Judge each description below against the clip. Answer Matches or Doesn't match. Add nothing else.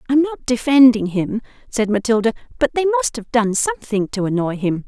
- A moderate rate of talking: Matches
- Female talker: Matches